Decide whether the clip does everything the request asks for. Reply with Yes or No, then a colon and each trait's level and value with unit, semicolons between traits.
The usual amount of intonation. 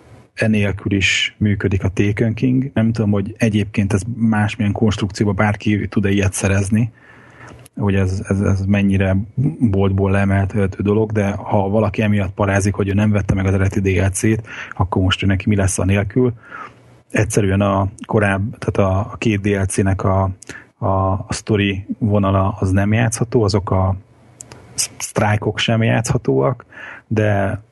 No: narrow, 2.2 semitones